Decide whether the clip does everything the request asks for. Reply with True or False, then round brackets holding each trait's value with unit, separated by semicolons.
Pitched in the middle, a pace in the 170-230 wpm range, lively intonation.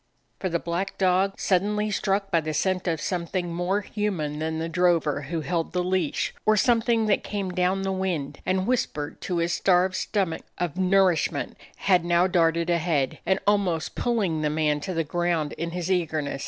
False (180 Hz; 180 wpm; 2.8 semitones)